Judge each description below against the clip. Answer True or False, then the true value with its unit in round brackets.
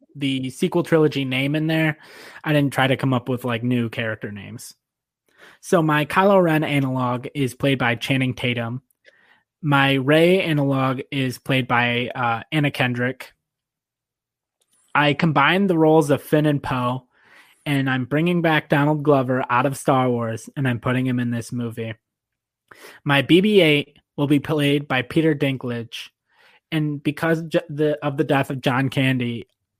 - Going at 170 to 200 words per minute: False (160 wpm)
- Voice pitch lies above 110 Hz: True (135 Hz)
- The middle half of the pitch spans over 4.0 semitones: False (3.4 semitones)